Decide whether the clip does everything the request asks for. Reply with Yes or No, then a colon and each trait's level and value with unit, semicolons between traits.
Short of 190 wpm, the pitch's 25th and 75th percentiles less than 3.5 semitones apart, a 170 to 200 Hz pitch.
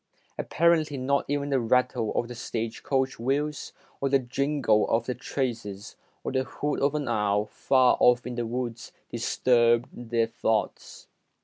No: average, 155 wpm; average, 3.0 semitones; low, 125 Hz